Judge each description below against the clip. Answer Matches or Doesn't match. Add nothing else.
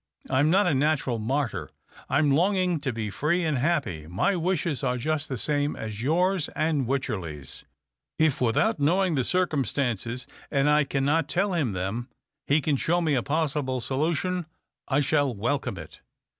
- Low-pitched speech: Doesn't match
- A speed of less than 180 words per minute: Matches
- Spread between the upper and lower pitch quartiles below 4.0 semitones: Doesn't match